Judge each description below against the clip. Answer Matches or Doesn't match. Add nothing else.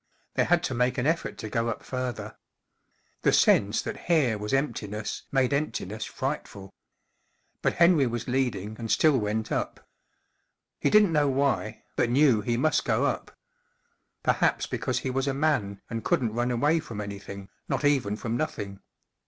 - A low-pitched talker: Matches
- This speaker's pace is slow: Doesn't match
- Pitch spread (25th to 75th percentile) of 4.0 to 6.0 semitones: Matches